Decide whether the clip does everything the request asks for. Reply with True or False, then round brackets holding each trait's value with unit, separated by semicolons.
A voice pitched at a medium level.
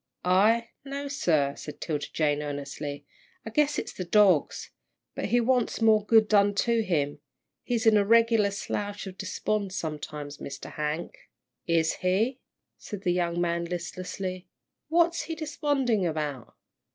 False (195 Hz)